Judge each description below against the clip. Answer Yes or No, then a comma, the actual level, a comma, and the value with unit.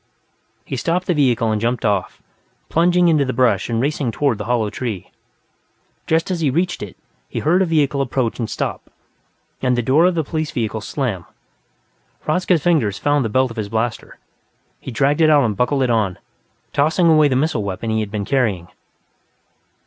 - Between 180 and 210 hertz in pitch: No, low, 130 Hz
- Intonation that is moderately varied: No, wide, 5.8 semitones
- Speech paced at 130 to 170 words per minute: No, average, 185 wpm